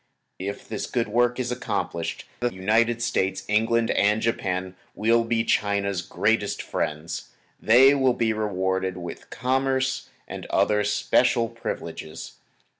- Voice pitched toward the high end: No, low, 110 Hz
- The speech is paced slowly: Yes, slow, 125 wpm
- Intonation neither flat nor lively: Yes, average, 3.6 semitones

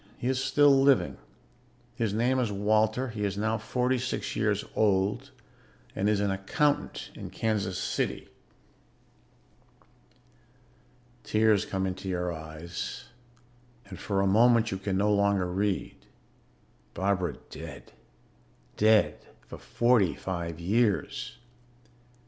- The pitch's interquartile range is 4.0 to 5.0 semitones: No, average, 3.6 semitones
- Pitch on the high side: No, low, 105 Hz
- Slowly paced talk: Yes, slow, 115 wpm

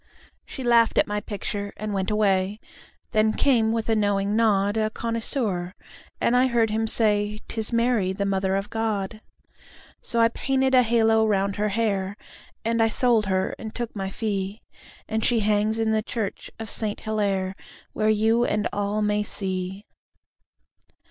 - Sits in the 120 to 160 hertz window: No, high, 215 Hz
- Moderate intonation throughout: No, narrow, 2.0 semitones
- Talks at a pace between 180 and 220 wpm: No, average, 165 wpm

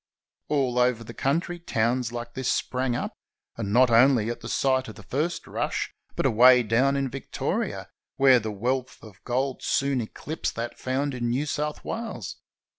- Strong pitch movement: No, narrow, 2.6 semitones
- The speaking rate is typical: Yes, average, 175 wpm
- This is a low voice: Yes, low, 125 Hz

